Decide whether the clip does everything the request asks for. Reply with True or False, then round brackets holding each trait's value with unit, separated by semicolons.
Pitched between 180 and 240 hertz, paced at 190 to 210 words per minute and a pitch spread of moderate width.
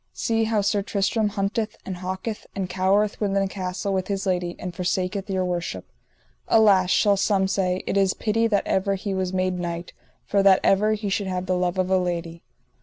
False (190 Hz; 200 wpm; 1.8 semitones)